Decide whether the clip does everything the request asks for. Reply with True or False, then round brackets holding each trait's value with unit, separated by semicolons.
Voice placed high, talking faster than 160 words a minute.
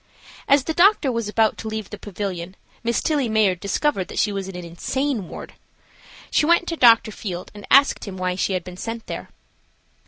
True (215 Hz; 200 wpm)